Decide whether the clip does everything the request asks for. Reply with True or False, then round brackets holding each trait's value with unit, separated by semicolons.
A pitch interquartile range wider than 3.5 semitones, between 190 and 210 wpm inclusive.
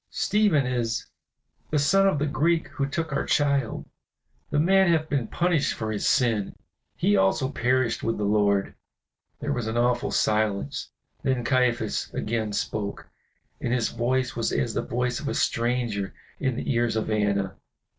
False (4.5 semitones; 165 wpm)